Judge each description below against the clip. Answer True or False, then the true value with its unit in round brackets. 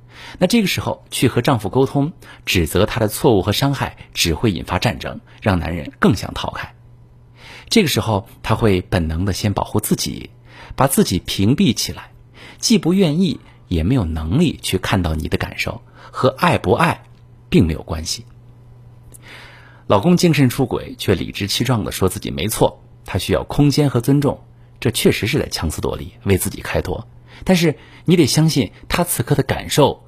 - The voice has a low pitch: True (120 Hz)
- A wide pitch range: False (4.8 semitones)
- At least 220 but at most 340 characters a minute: True (260 characters per minute)